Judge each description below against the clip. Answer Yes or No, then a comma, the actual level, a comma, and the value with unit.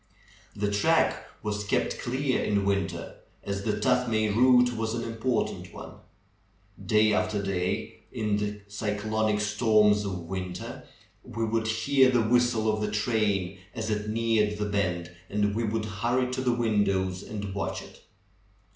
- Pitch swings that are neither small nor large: No, narrow, 1.9 semitones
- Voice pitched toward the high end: No, low, 105 Hz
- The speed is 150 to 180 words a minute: Yes, average, 155 wpm